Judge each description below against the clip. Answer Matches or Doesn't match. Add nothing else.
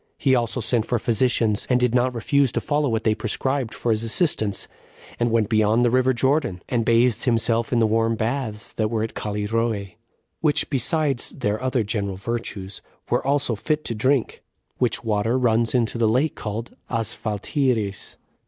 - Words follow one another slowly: Doesn't match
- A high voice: Doesn't match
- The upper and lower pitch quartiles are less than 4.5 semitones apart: Matches